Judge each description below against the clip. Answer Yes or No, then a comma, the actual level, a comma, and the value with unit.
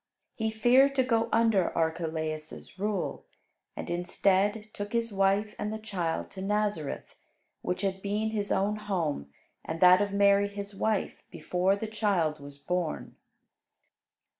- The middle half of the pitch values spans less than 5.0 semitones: Yes, average, 3.1 semitones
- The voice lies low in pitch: No, high, 200 Hz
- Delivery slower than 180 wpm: Yes, average, 140 wpm